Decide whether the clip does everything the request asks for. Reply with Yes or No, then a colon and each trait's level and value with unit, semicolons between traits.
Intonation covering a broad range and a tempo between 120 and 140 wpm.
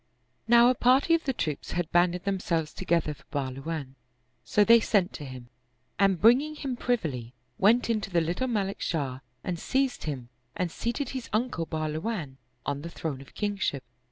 No: wide, 7.4 semitones; average, 180 wpm